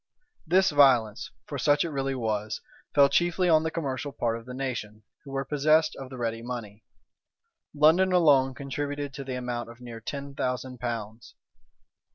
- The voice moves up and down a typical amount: Yes, average, 3.5 semitones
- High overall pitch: No, low, 135 Hz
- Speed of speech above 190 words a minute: No, average, 170 wpm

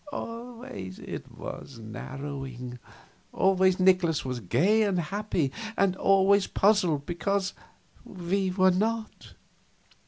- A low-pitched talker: No, medium, 185 Hz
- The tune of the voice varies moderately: No, wide, 5.9 semitones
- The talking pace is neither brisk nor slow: No, slow, 100 wpm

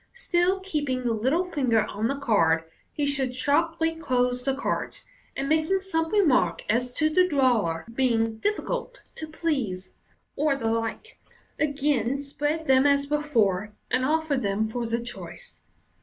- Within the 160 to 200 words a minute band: No, average, 150 wpm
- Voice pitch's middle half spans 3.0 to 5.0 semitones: No, wide, 5.4 semitones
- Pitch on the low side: No, very high, 275 Hz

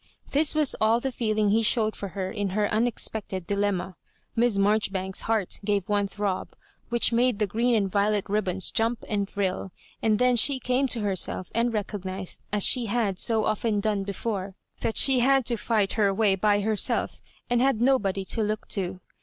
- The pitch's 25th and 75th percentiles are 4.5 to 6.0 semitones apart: No, average, 2.8 semitones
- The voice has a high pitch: Yes, high, 210 Hz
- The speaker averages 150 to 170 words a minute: No, average, 185 wpm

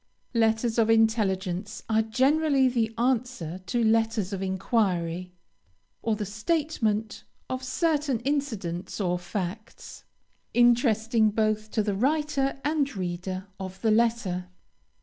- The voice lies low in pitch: No, high, 220 Hz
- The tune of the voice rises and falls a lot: No, average, 4.2 semitones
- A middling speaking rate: No, slow, 115 wpm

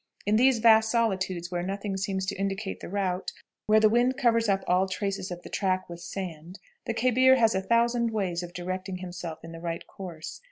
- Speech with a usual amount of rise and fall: Yes, average, 3.6 semitones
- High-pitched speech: Yes, high, 195 Hz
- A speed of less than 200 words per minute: No, fast, 205 wpm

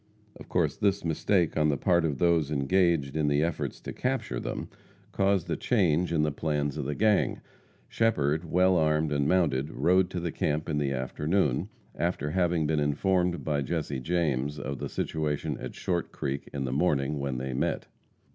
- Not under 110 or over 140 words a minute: No, average, 185 wpm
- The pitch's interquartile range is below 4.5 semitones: Yes, average, 3.5 semitones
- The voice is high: No, very low, 75 Hz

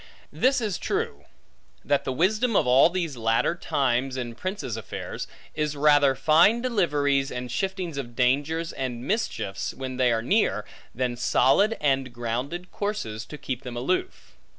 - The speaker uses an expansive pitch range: Yes, wide, 6.7 semitones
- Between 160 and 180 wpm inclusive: No, average, 150 wpm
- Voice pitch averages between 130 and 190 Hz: Yes, medium, 140 Hz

